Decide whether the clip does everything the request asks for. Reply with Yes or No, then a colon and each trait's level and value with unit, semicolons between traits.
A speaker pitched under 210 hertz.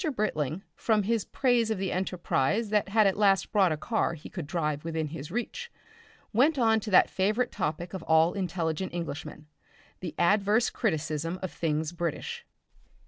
Yes: medium, 185 Hz